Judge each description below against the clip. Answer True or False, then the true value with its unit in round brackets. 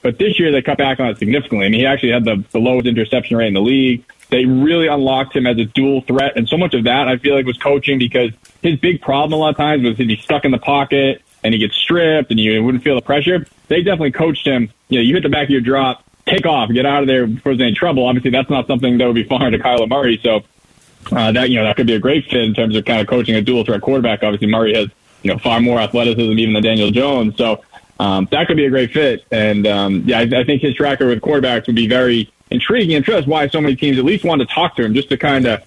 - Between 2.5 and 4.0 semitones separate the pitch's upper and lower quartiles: True (3.4 semitones)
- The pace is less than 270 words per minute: False (290 wpm)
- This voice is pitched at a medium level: False (125 Hz)